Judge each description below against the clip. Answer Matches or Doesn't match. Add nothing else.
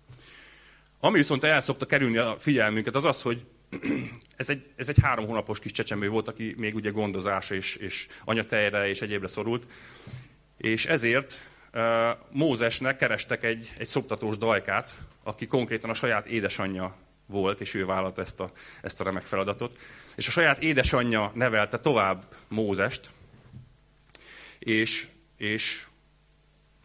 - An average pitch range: Matches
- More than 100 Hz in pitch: Matches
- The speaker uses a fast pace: Doesn't match